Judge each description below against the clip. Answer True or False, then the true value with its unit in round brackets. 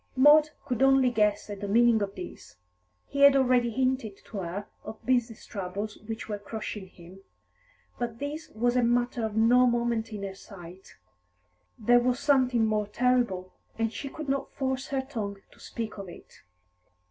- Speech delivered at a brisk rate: False (170 wpm)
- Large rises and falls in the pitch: False (3.6 semitones)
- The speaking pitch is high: True (230 Hz)